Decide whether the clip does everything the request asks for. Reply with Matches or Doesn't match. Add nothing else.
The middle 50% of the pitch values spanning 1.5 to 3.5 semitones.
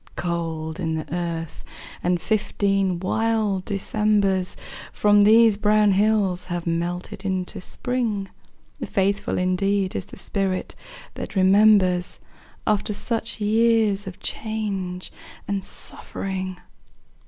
Matches